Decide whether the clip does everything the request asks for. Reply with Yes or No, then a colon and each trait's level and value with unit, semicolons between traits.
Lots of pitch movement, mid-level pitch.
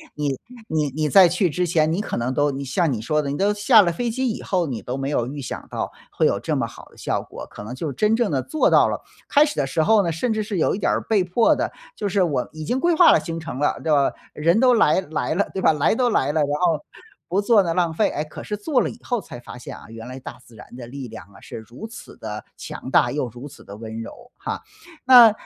Yes: wide, 7.5 semitones; medium, 160 Hz